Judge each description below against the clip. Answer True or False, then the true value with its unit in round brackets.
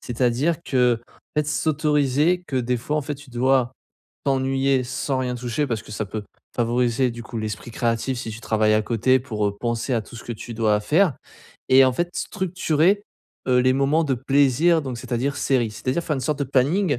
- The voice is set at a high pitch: False (130 Hz)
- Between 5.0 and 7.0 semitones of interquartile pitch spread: False (3.5 semitones)